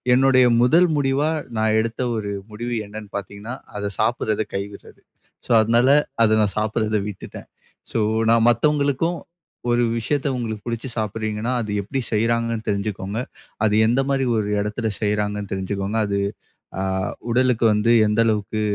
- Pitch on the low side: Yes, low, 110 Hz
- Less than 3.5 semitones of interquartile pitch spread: Yes, narrow, 2.6 semitones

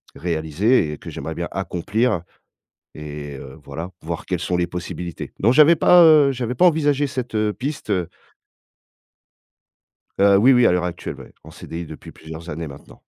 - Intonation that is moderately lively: No, wide, 7.7 semitones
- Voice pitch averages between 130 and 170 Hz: No, very low, 90 Hz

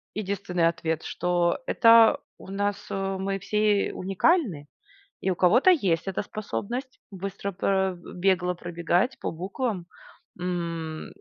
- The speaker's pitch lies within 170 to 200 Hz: Yes, high, 190 Hz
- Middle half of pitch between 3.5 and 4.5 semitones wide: No, narrow, 2.6 semitones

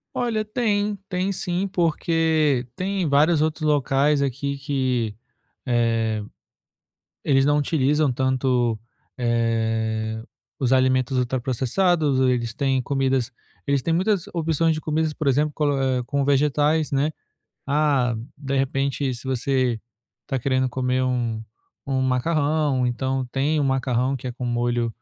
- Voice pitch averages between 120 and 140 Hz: Yes, low, 135 Hz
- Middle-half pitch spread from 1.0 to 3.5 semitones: Yes, average, 3.2 semitones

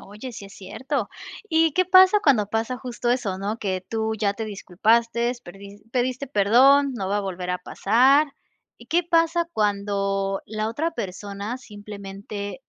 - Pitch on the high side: Yes, high, 220 Hz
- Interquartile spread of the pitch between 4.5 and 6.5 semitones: Yes, average, 4.8 semitones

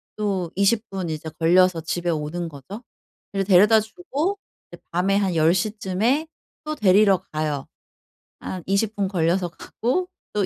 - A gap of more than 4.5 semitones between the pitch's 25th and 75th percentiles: No, average, 3.8 semitones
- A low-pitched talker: No, high, 190 Hz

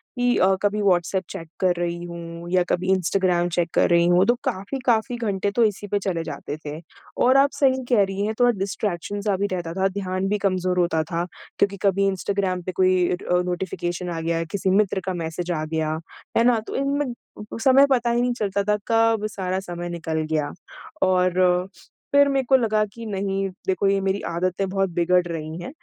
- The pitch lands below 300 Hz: Yes, high, 190 Hz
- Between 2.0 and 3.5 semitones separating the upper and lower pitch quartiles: Yes, average, 3.2 semitones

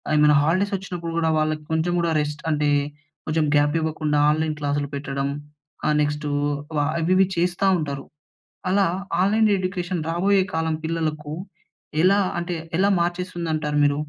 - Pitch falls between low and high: Yes, medium, 160 Hz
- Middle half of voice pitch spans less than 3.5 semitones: Yes, average, 3.0 semitones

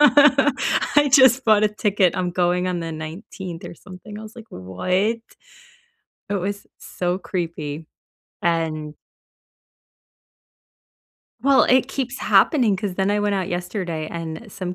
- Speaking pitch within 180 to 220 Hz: Yes, high, 190 Hz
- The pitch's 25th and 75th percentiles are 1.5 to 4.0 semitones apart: No, average, 4.4 semitones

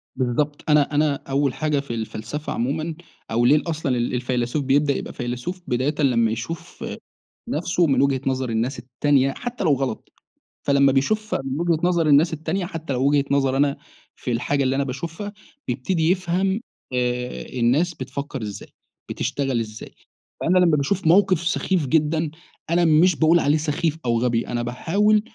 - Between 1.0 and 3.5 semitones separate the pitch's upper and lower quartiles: No, average, 4.5 semitones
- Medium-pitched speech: Yes, medium, 145 Hz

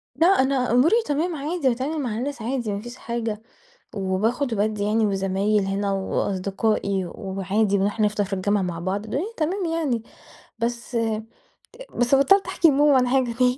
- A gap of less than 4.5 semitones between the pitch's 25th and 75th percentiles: No, average, 5.1 semitones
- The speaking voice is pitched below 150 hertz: No, high, 230 Hz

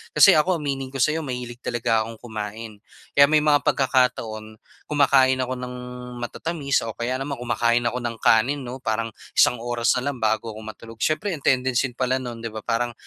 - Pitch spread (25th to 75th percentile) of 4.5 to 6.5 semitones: No, average, 2.9 semitones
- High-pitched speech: No, low, 125 Hz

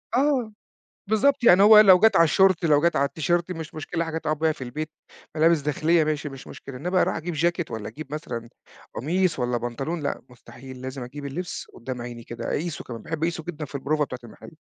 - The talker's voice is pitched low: No, medium, 155 Hz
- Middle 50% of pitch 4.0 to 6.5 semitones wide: Yes, average, 4.5 semitones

